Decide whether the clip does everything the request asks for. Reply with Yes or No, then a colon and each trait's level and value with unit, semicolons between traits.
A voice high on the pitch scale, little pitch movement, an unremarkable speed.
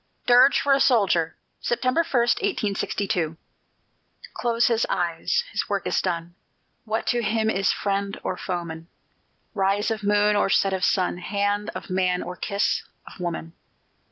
No: high, 200 Hz; average, 3.9 semitones; average, 150 wpm